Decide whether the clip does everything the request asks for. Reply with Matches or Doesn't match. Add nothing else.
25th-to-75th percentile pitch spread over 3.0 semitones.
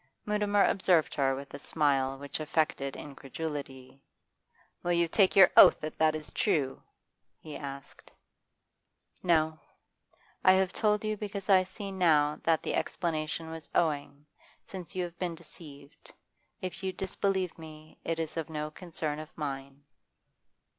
Matches